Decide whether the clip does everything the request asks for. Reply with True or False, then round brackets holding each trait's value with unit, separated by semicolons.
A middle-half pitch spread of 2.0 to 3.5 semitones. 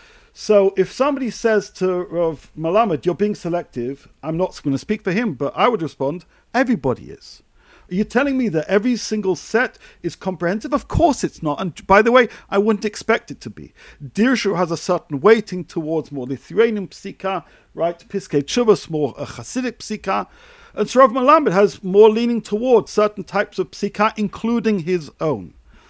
False (5.2 semitones)